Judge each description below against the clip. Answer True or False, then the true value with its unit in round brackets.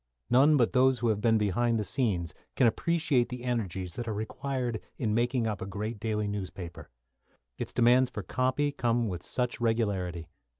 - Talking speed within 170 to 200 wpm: True (175 wpm)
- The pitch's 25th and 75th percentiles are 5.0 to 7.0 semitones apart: False (3.4 semitones)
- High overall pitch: False (115 Hz)